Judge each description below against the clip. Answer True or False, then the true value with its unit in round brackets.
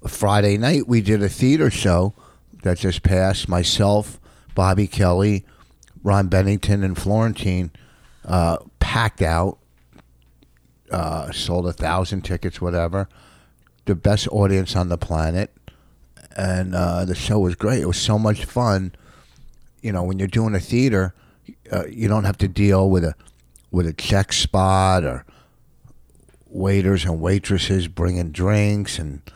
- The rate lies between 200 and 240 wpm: False (140 wpm)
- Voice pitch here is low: True (95 Hz)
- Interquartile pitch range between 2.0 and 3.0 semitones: True (2.7 semitones)